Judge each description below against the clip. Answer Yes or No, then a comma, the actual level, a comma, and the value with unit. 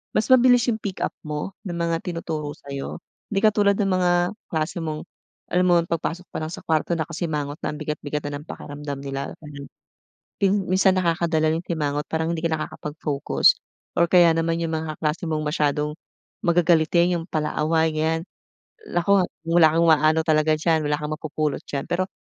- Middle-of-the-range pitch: Yes, medium, 160 Hz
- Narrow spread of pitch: Yes, narrow, 2.3 semitones